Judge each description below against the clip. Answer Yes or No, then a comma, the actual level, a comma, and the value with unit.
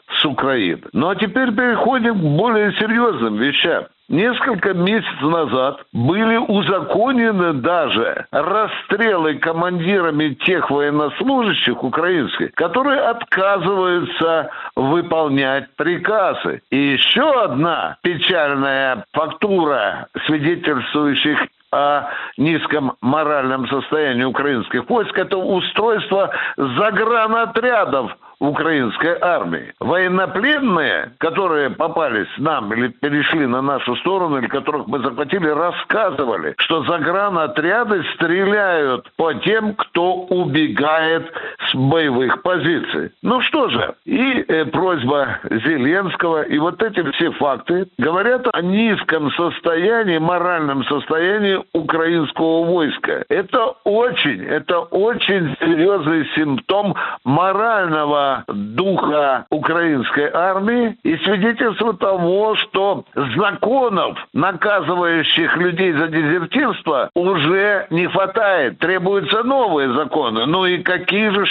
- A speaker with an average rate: No, slow, 95 wpm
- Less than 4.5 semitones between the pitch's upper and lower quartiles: No, average, 5.1 semitones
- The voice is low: No, medium, 175 Hz